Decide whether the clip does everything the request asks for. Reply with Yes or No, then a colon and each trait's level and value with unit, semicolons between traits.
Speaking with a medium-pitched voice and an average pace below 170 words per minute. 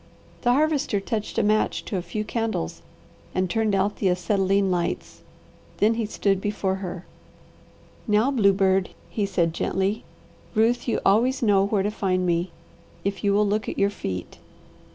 No: high, 200 Hz; average, 160 wpm